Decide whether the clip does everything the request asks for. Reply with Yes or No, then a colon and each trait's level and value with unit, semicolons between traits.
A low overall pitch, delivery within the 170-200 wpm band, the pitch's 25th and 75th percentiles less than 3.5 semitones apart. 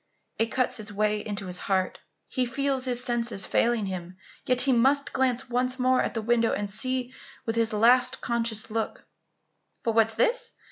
No: high, 235 Hz; average, 185 wpm; average, 2.9 semitones